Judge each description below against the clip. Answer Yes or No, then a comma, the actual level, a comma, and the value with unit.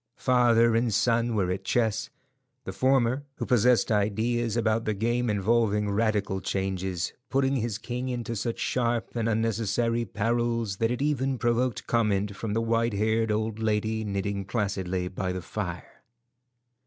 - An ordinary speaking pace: Yes, average, 150 wpm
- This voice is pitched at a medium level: No, low, 115 Hz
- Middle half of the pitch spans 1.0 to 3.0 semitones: Yes, narrow, 2.5 semitones